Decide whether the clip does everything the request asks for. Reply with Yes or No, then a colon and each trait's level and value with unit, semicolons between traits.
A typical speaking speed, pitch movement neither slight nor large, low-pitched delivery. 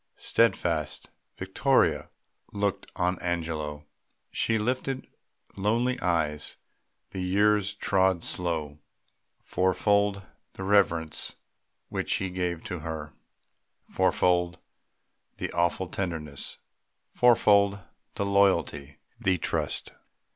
No: slow, 90 wpm; average, 3.5 semitones; very low, 90 Hz